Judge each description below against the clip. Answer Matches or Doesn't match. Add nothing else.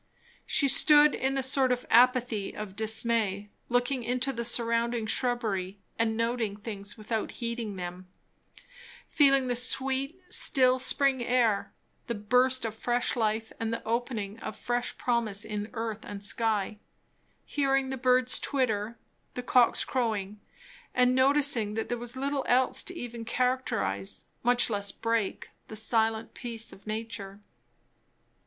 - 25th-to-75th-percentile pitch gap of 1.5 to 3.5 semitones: Matches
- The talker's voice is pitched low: Doesn't match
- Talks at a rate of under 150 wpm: Matches